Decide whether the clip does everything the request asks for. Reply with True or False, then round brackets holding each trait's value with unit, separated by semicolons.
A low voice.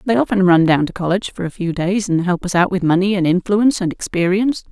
False (185 Hz)